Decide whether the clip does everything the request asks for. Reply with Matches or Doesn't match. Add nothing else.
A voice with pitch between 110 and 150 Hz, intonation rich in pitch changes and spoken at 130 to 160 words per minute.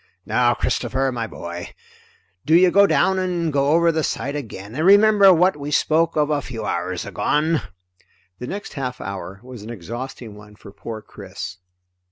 Doesn't match